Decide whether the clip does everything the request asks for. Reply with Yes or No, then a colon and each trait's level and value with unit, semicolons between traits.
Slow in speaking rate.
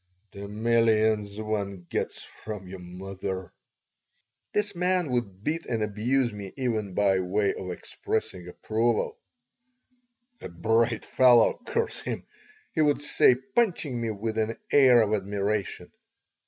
Yes: slow, 130 wpm